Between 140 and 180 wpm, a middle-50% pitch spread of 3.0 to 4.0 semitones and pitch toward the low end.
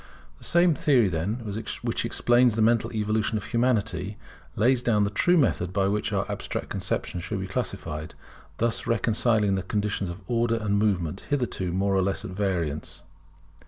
Yes: average, 165 wpm; average, 3.4 semitones; low, 105 Hz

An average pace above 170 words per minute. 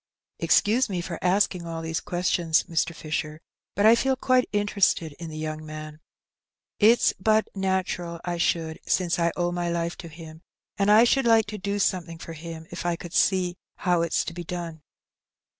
Yes: average, 185 wpm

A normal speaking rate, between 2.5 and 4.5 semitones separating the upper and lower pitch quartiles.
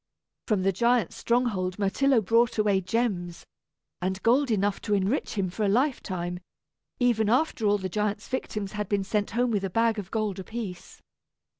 Yes: average, 170 wpm; average, 3.4 semitones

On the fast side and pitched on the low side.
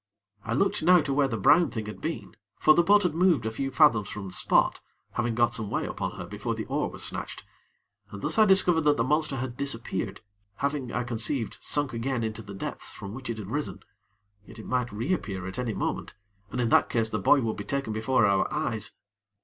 Yes: fast, 230 wpm; low, 120 Hz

